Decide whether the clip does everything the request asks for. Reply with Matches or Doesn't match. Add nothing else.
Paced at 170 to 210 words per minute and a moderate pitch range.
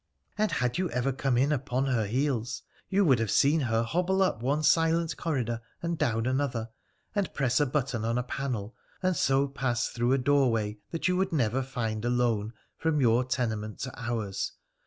Matches